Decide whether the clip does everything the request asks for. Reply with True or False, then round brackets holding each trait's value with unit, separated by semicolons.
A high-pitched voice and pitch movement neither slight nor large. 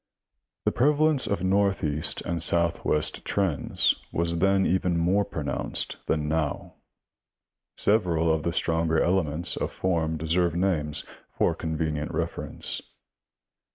False (85 Hz; 3.0 semitones)